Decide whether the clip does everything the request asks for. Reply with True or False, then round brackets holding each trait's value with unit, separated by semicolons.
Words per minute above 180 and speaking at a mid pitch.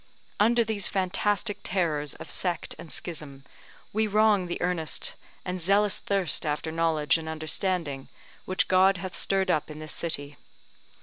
False (145 wpm; 180 Hz)